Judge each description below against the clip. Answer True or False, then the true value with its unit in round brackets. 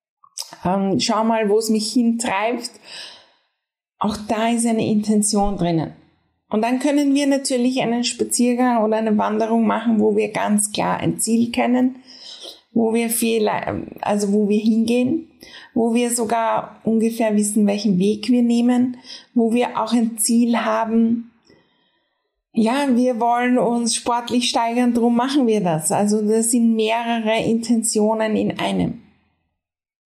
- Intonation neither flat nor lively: False (1.9 semitones)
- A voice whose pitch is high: True (230 Hz)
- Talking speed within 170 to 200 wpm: False (140 wpm)